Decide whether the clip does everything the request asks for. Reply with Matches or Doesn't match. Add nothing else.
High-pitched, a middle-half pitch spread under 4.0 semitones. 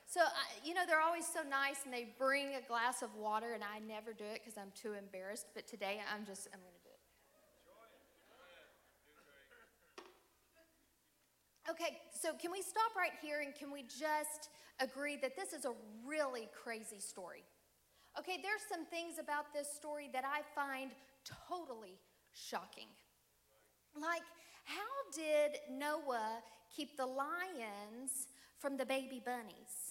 Doesn't match